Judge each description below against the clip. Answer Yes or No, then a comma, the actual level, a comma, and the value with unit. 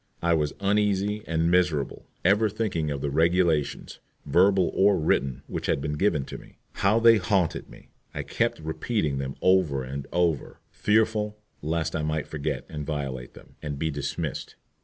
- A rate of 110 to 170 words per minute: Yes, average, 160 wpm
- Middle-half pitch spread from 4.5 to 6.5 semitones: Yes, average, 5.2 semitones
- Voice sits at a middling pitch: No, very low, 80 Hz